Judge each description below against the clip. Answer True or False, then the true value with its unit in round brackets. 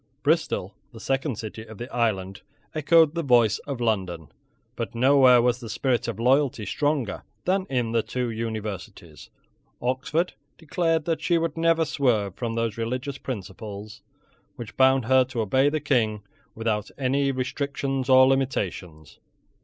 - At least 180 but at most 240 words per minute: False (145 wpm)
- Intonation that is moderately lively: True (4.1 semitones)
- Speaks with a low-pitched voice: True (125 Hz)